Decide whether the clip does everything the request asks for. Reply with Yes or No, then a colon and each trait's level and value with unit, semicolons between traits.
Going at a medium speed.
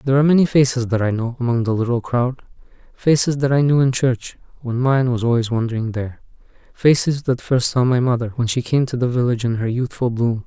No: fast, 225 wpm